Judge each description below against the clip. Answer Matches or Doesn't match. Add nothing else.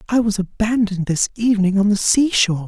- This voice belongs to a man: Matches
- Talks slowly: Doesn't match